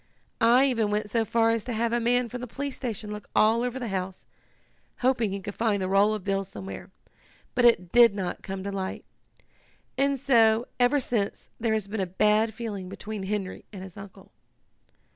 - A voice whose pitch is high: Yes, high, 215 Hz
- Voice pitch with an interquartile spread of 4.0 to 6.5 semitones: No, average, 3.2 semitones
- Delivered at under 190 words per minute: No, average, 200 wpm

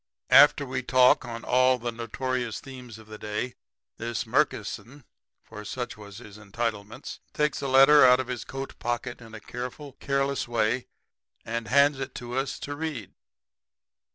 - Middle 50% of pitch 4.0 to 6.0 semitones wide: No, average, 2.9 semitones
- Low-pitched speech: Yes, low, 125 Hz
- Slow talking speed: No, average, 165 wpm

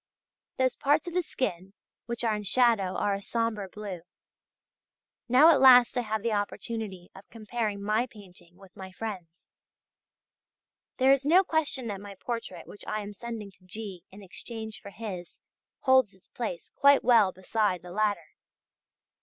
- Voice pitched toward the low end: No, high, 215 Hz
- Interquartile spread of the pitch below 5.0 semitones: Yes, average, 3.8 semitones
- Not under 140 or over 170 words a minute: Yes, average, 160 wpm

